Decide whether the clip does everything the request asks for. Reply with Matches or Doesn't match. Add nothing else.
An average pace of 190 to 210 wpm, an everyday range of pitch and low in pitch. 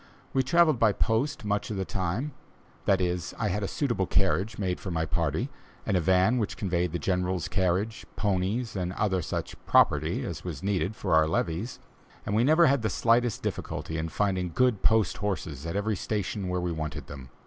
Matches